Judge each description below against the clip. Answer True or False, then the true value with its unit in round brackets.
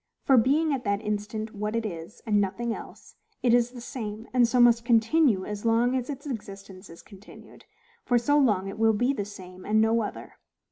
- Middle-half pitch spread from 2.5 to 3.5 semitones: True (3.0 semitones)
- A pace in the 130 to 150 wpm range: False (205 wpm)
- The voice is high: True (225 Hz)